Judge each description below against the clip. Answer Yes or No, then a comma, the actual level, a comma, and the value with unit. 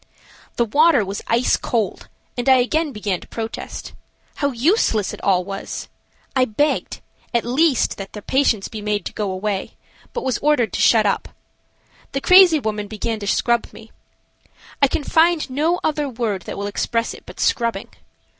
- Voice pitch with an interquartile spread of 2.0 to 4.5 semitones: No, average, 5.3 semitones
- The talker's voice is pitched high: Yes, high, 235 Hz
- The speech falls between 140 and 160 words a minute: No, average, 175 wpm